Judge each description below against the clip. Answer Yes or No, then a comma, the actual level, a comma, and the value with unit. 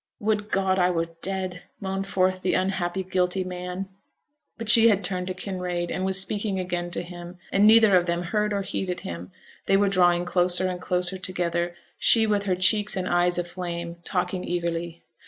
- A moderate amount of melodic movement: No, narrow, 1.7 semitones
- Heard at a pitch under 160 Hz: No, medium, 185 Hz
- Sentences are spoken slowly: No, average, 185 wpm